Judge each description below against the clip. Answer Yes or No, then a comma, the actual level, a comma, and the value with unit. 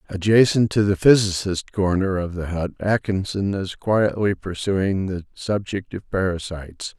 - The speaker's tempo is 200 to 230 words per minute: No, slow, 135 wpm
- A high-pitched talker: No, very low, 95 Hz